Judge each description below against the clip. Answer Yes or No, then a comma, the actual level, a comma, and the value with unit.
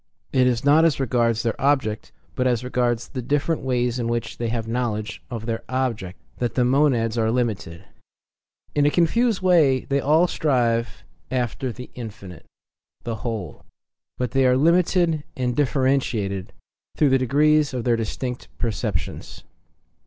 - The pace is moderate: Yes, average, 155 wpm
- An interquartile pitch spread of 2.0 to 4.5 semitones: Yes, average, 3.4 semitones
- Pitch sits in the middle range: No, low, 125 Hz